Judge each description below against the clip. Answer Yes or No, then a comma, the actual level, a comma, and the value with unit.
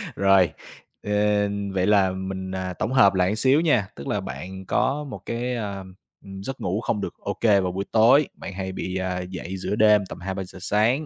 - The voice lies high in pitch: No, low, 100 Hz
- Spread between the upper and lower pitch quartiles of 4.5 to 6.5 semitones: No, average, 2.9 semitones